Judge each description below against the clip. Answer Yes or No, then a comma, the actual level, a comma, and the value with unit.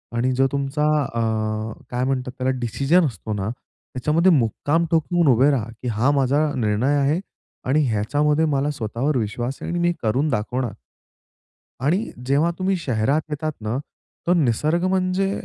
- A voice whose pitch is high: No, low, 135 Hz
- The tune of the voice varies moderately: Yes, average, 4.9 semitones